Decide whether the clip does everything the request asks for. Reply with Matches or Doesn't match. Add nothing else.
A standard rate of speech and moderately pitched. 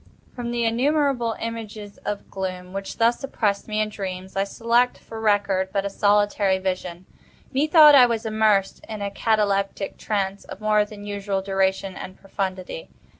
Doesn't match